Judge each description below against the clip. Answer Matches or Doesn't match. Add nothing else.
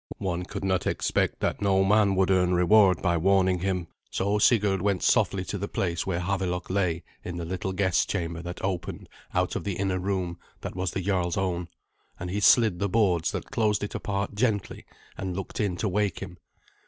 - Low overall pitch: Matches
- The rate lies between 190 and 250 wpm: Matches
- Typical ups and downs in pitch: Doesn't match